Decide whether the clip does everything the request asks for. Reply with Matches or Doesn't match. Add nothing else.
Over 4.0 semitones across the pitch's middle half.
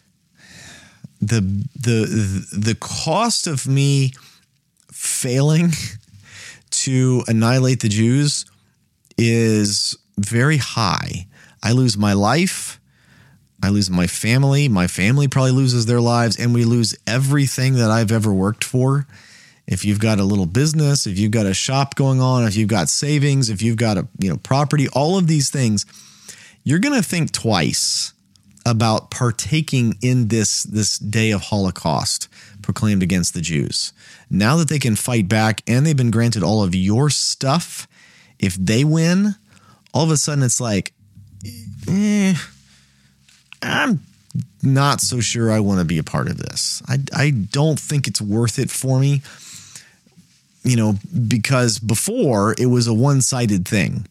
Matches